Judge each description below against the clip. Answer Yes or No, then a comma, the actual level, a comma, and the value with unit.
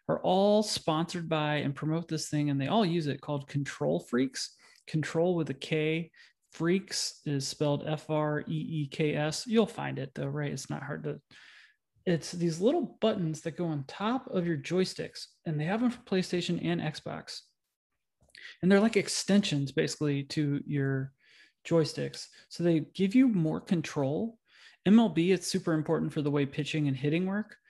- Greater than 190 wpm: No, average, 180 wpm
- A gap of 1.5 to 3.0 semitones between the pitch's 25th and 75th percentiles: No, average, 3.8 semitones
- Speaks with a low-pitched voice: No, medium, 160 Hz